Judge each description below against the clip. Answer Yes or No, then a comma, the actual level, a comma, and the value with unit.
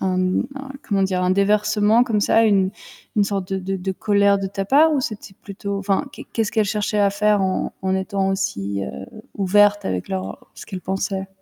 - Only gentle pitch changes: Yes, narrow, 1.7 semitones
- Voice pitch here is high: Yes, high, 200 Hz